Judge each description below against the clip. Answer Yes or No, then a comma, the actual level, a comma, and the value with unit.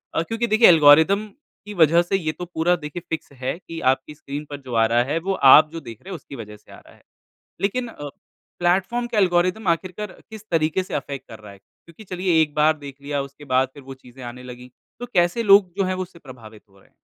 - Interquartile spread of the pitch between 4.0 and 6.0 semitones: Yes, wide, 5.6 semitones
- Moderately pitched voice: Yes, medium, 160 Hz